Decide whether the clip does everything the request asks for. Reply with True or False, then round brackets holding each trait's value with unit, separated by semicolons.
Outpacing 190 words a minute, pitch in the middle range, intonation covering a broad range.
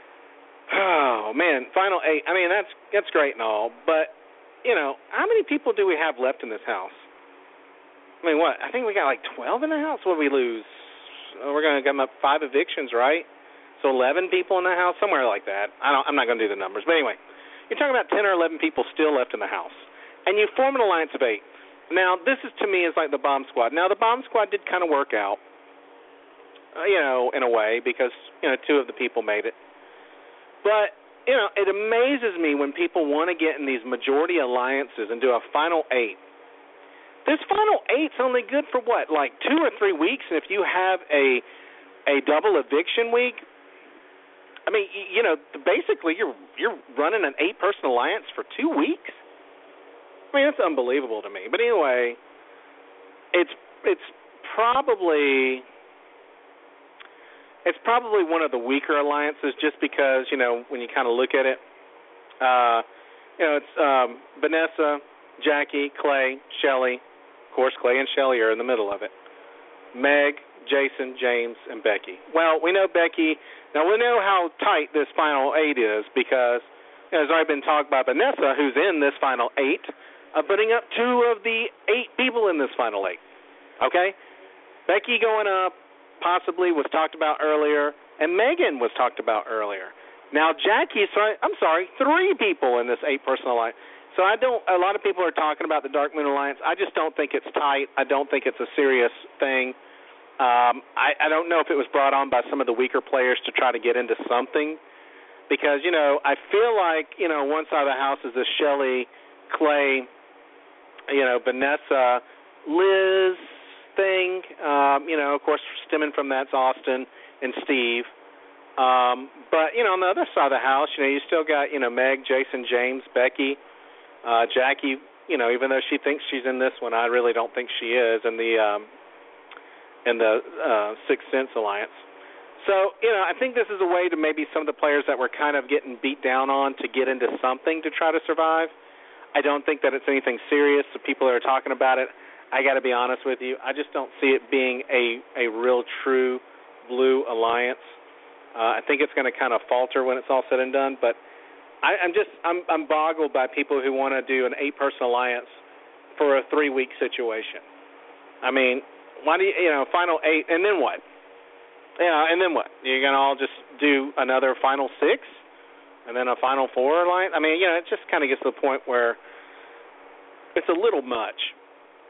True (200 wpm; 145 Hz; 5.9 semitones)